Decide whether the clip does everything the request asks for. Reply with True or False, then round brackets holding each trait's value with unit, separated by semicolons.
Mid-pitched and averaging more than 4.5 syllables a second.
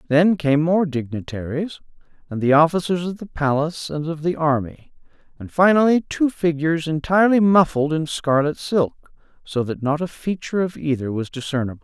True (155 Hz; 5.3 syllables/s)